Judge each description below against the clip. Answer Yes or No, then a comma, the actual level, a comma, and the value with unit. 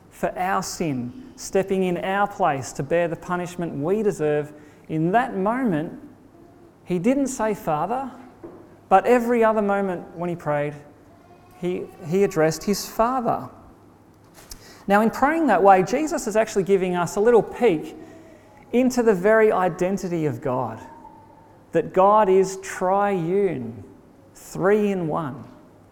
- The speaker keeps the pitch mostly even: No, average, 4.5 semitones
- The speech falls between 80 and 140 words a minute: Yes, slow, 135 wpm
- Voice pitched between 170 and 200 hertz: Yes, high, 190 Hz